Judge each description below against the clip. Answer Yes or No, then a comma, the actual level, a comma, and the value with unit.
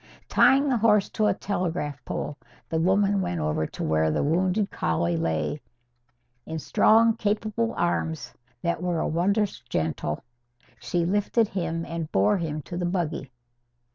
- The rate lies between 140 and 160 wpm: Yes, average, 145 wpm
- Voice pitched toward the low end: No, medium, 170 Hz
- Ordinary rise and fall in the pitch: No, wide, 5.8 semitones